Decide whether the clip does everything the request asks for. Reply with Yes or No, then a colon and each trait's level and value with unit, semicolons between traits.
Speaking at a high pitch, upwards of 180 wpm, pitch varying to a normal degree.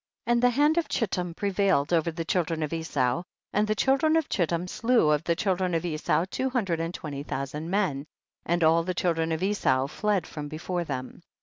No: medium, 170 Hz; fast, 205 wpm; average, 4.3 semitones